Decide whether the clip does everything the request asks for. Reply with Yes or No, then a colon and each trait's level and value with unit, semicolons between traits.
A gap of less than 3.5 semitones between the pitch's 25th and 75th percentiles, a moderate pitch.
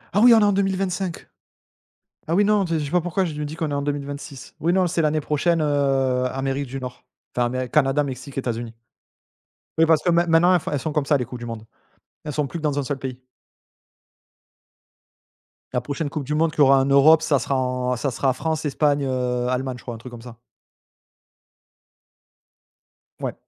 No: average, 3.8 semitones; medium, 145 Hz